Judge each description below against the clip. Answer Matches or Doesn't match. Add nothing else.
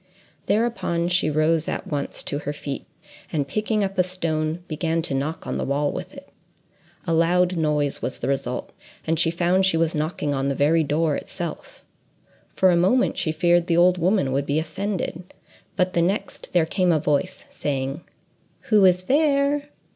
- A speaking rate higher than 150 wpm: Matches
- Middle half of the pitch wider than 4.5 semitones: Doesn't match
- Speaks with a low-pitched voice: Doesn't match